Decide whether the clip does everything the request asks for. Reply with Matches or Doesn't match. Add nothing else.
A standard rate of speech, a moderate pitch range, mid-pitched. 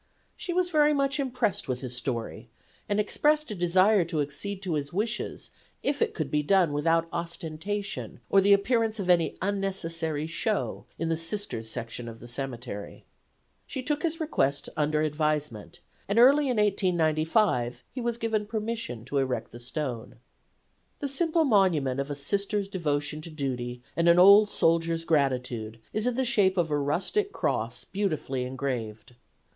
Doesn't match